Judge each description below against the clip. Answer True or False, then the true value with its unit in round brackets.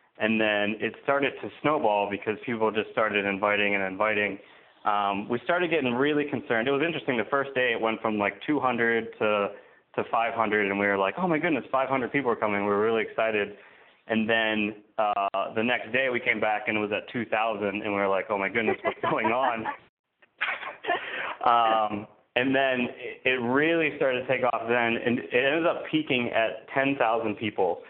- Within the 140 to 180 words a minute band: False (205 wpm)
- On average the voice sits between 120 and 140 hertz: False (110 Hz)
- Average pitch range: True (3.7 semitones)